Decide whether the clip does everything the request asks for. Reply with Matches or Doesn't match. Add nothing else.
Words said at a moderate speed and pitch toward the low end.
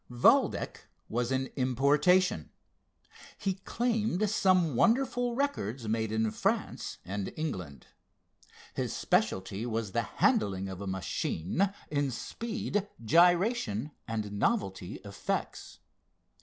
Doesn't match